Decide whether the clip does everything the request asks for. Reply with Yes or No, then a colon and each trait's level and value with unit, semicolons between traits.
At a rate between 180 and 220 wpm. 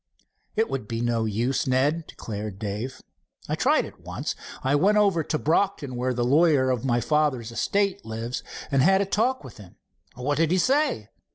Yes: average, 185 wpm